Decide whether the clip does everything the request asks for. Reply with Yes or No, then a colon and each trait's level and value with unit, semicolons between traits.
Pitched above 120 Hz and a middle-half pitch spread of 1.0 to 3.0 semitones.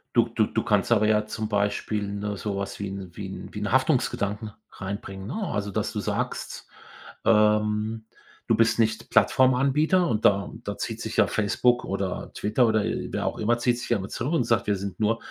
No: low, 105 Hz; narrow, 2.6 semitones